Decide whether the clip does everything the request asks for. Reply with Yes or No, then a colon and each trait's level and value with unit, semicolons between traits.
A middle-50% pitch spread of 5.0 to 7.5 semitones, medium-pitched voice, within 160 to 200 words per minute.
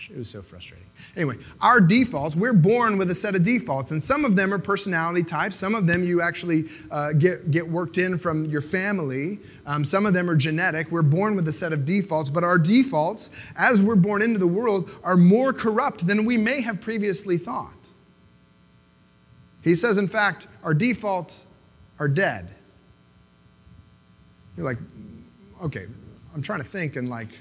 Yes: average, 5.3 semitones; medium, 175 Hz; average, 180 wpm